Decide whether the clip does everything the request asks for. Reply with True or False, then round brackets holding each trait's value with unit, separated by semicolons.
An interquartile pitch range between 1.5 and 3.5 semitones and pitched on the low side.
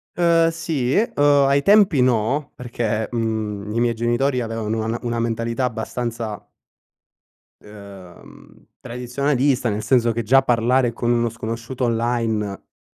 True (2.8 semitones; 120 Hz)